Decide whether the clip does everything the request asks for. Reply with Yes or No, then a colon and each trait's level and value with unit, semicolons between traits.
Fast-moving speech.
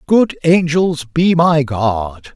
No: slow, 130 wpm